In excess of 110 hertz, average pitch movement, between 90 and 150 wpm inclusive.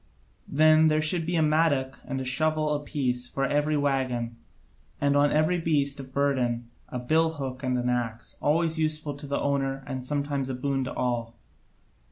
No: medium, 140 Hz; average, 3.1 semitones; average, 175 wpm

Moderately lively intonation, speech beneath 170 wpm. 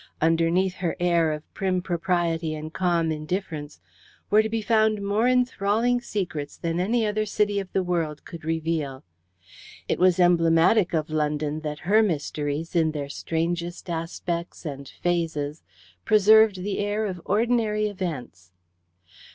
Yes: average, 4.4 semitones; average, 140 wpm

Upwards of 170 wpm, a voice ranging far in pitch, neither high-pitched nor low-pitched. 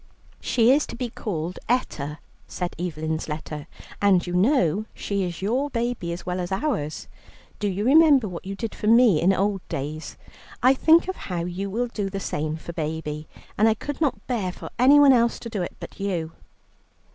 No: average, 190 wpm; wide, 6.0 semitones; high, 195 Hz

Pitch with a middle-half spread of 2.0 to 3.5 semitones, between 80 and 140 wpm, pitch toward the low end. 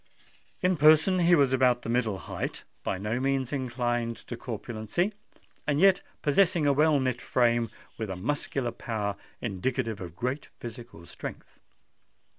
No: average, 4.3 semitones; slow, 135 wpm; low, 125 Hz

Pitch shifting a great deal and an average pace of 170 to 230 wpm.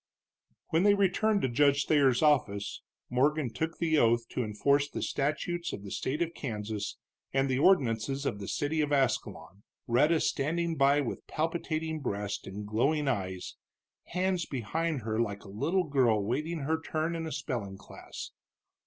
No: wide, 5.9 semitones; average, 160 wpm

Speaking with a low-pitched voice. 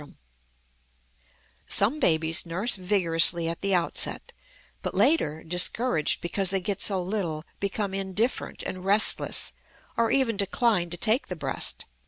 No: high, 190 Hz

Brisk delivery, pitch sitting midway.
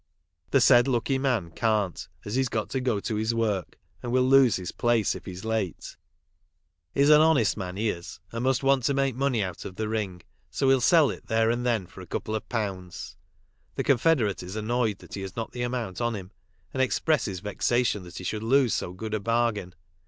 No: fast, 220 wpm; low, 115 Hz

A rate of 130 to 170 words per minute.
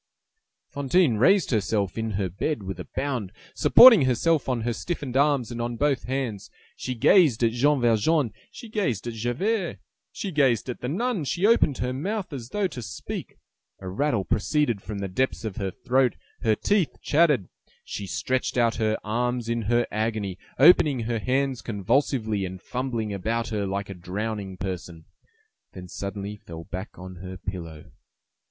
Yes: average, 165 wpm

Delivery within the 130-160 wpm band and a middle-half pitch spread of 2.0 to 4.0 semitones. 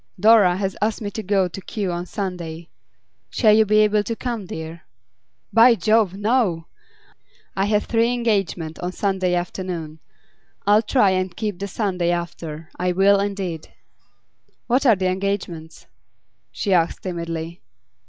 Yes: average, 145 wpm; average, 3.4 semitones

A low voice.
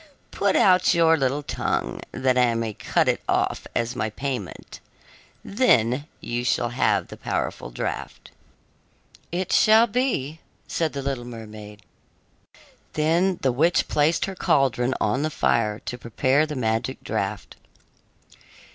Yes: low, 130 Hz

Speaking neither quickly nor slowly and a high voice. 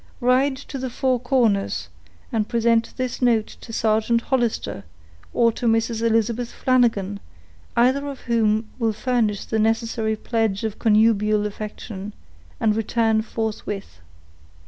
No: slow, 125 wpm; high, 225 Hz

